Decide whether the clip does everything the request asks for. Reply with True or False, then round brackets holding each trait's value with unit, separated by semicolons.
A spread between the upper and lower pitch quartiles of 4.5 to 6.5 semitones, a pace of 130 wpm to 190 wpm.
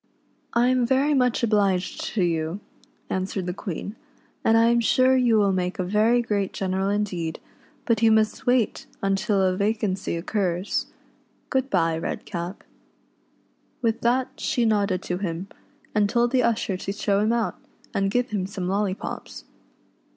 False (3.9 semitones; 160 wpm)